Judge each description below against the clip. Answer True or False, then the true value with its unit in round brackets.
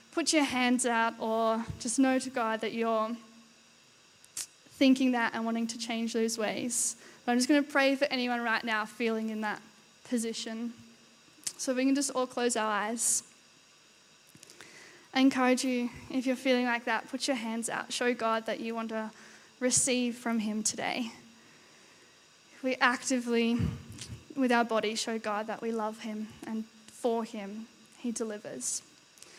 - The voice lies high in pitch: True (235 Hz)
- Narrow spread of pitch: True (2.2 semitones)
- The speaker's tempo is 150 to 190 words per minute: True (165 wpm)